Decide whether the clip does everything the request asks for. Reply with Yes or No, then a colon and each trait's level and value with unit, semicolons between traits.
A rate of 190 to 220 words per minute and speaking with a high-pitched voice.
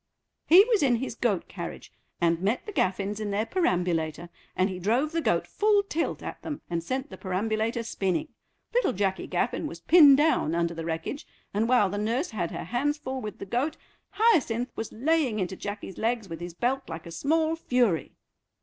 Yes: average, 195 wpm; high, 225 Hz